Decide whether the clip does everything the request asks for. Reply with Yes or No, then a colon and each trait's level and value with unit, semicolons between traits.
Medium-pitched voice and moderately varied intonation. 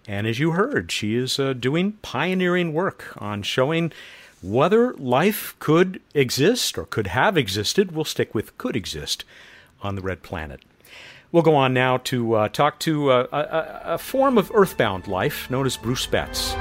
No: medium, 145 Hz; wide, 6.4 semitones